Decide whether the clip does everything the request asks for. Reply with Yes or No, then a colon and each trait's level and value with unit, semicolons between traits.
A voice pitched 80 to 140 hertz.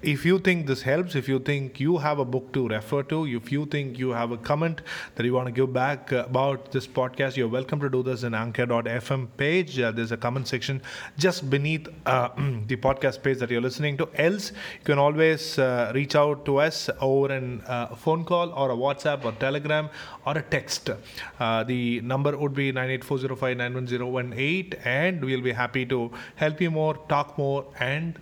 Yes: low, 135 Hz